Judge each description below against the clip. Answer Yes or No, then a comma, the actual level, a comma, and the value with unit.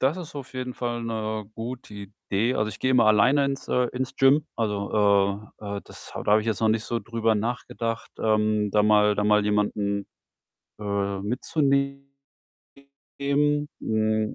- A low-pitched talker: Yes, low, 110 Hz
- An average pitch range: Yes, average, 3.6 semitones